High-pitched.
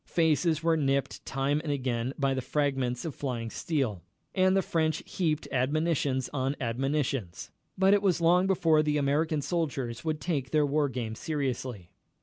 No: medium, 145 Hz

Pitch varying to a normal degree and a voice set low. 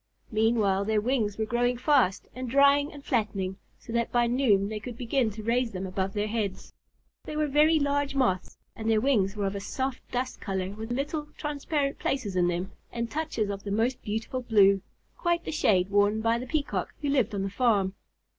No: average, 5.0 semitones; high, 230 Hz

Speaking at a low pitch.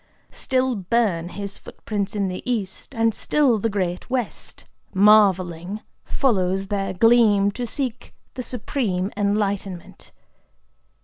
No: high, 205 Hz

